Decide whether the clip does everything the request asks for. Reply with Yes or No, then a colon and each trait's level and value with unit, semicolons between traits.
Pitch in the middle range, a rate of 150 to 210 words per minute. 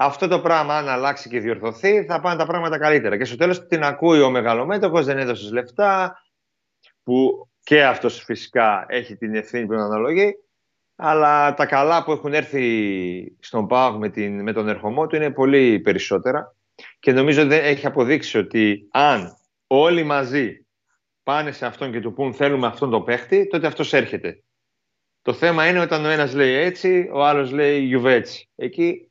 Yes: medium, 145 Hz; fast, 170 wpm